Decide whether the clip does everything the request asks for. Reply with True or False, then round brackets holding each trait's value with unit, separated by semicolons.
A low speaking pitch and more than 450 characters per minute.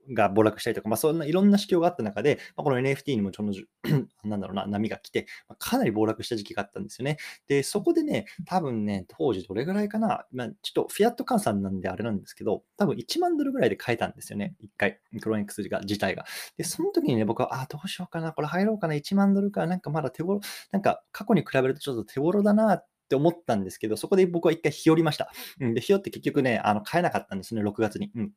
False (155 Hz; 505 characters per minute)